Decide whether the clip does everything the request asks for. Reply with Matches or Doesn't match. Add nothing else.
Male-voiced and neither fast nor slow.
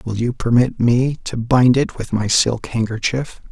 Matches